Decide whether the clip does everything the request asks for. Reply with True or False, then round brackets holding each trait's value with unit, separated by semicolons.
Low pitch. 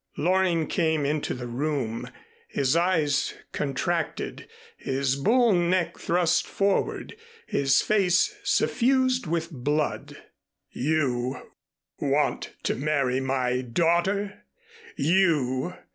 False (155 Hz)